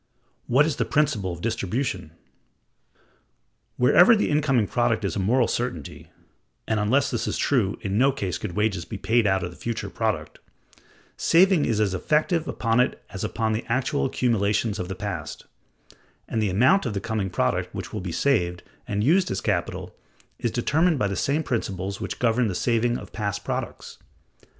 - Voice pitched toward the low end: Yes, low, 110 Hz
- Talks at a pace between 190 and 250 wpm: No, average, 180 wpm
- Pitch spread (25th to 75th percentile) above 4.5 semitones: Yes, average, 5.1 semitones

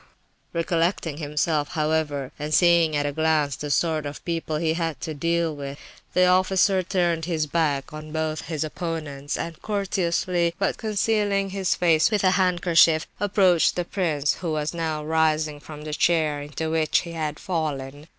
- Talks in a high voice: No, medium, 160 Hz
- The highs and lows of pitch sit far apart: No, narrow, 2.5 semitones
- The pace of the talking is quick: No, average, 170 wpm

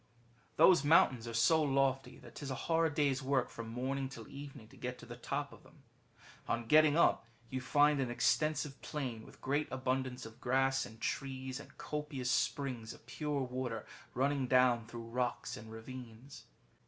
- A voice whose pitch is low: Yes, low, 130 Hz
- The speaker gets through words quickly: No, average, 180 wpm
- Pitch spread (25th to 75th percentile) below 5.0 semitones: Yes, average, 2.8 semitones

